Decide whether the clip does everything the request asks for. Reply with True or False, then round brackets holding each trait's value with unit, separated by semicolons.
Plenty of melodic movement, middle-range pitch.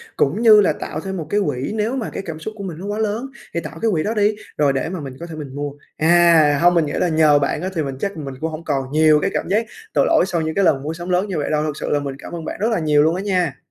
False (4.8 semitones; 165 Hz)